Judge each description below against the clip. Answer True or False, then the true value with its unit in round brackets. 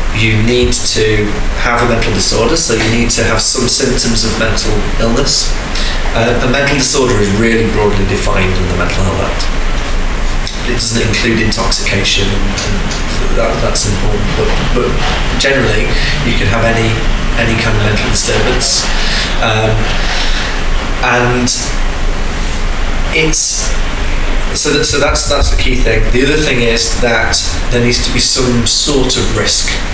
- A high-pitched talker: False (110 Hz)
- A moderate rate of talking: True (150 wpm)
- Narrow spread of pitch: False (3.4 semitones)